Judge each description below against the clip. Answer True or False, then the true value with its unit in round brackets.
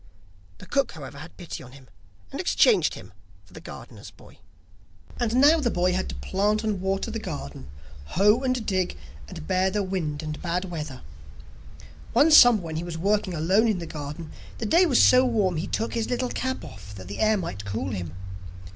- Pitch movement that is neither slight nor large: False (6.5 semitones)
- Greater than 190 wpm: True (200 wpm)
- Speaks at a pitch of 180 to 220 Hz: True (185 Hz)